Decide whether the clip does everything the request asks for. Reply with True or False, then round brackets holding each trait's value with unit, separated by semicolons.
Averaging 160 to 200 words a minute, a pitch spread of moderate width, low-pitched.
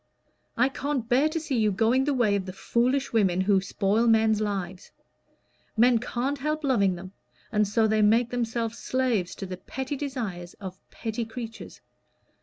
False (170 wpm; 4.1 semitones; 225 Hz)